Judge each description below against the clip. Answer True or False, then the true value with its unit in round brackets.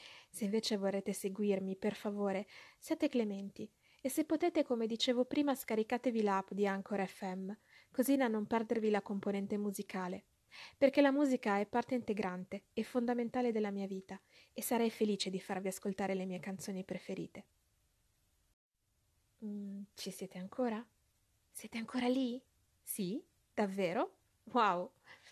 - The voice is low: False (210 Hz)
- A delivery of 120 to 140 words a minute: True (135 wpm)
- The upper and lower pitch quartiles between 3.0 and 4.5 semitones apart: True (4.0 semitones)